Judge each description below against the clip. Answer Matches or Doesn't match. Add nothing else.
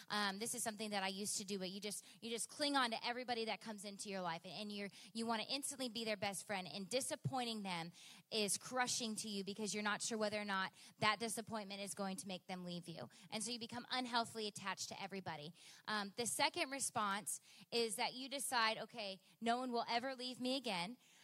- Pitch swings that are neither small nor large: Matches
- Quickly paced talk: Matches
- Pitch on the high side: Matches